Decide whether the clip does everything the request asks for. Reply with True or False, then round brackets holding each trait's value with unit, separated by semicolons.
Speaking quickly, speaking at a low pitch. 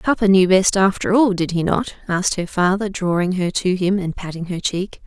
False (225 wpm; 185 Hz)